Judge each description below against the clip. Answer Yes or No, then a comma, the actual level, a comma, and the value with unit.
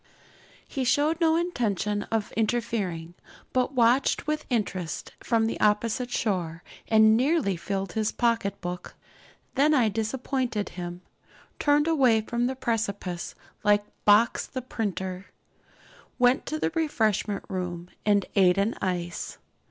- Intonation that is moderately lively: Yes, average, 4.7 semitones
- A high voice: Yes, high, 220 Hz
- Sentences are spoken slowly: Yes, slow, 130 wpm